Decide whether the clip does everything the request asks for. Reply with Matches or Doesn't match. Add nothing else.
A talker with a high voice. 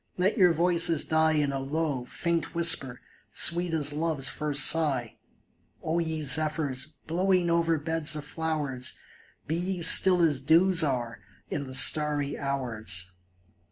Doesn't match